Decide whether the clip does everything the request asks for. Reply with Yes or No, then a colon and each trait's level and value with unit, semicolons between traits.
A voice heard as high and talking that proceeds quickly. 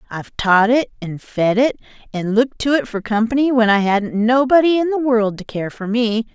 Yes: high, 230 Hz; fast, 220 wpm